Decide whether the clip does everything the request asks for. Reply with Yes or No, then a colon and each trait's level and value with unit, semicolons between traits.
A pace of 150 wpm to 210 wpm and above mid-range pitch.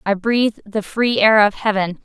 Yes: fast, 205 wpm; high, 210 Hz